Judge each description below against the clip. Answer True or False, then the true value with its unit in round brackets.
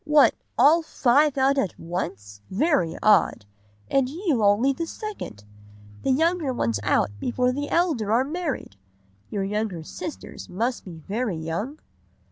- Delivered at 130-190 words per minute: True (140 wpm)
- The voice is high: True (250 Hz)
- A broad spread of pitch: True (8.1 semitones)